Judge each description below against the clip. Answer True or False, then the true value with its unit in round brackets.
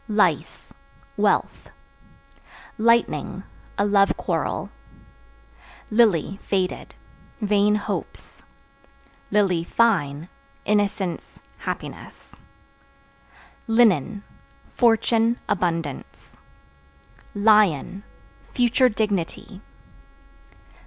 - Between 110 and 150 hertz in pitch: False (205 Hz)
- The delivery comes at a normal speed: False (55 wpm)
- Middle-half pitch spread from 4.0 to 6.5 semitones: False (3.5 semitones)